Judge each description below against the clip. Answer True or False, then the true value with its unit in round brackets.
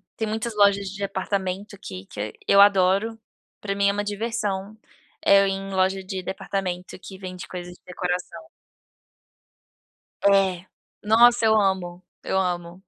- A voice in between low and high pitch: False (195 Hz)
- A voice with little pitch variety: True (2.0 semitones)